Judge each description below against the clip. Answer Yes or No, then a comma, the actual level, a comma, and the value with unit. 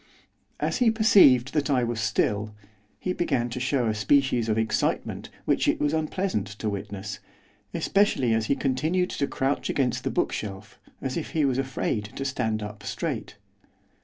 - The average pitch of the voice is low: Yes, low, 125 Hz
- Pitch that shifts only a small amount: No, average, 5.1 semitones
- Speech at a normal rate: Yes, average, 165 wpm